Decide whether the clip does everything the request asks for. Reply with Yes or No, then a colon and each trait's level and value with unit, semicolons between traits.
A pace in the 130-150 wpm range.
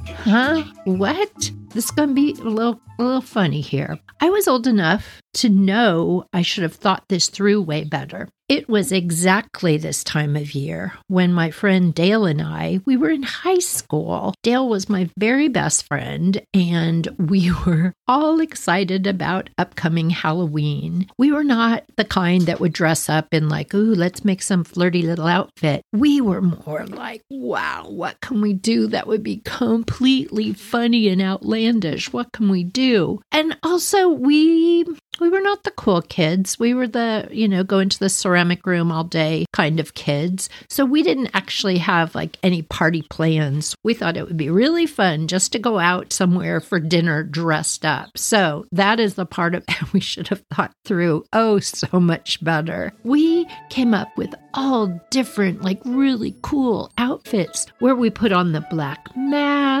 No: average, 180 wpm